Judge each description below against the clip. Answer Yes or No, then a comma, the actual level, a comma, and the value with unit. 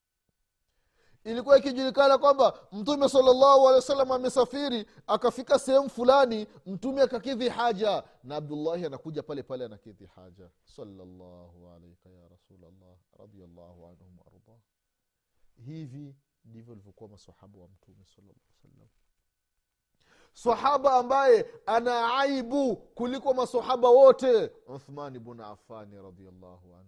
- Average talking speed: No, slow, 85 wpm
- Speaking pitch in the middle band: Yes, medium, 150 Hz